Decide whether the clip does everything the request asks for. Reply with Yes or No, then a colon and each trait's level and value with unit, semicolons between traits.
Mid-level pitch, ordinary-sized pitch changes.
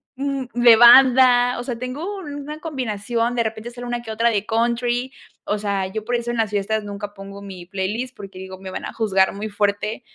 No: high, 230 Hz; average, 3.3 semitones